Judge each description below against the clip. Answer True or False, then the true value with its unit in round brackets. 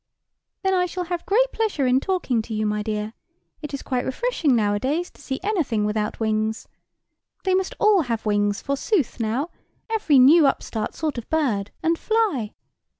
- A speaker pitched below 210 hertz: False (270 Hz)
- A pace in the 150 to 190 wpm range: True (170 wpm)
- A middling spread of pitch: False (8.6 semitones)